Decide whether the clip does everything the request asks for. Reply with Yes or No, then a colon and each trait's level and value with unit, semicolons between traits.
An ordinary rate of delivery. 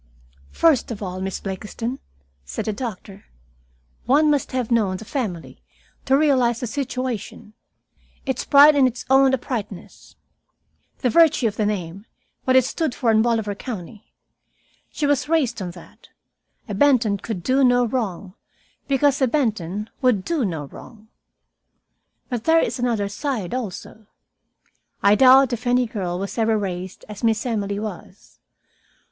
Yes: average, 150 wpm